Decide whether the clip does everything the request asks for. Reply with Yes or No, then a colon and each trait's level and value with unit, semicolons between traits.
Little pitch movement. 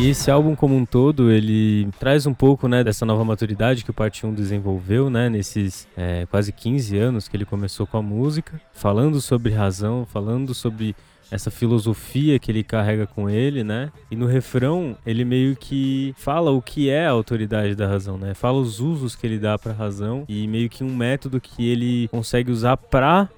No: average, 3.7 semitones